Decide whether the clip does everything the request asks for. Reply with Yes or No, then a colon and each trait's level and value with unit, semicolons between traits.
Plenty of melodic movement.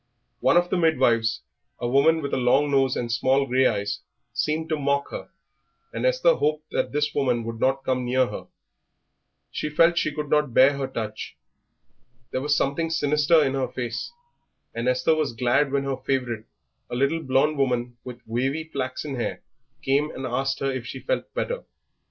No: average, 3.3 semitones